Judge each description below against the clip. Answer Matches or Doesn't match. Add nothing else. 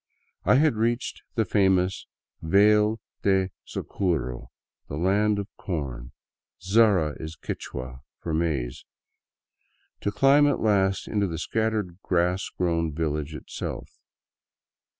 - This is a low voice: Matches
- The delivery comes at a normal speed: Doesn't match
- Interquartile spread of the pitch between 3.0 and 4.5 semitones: Doesn't match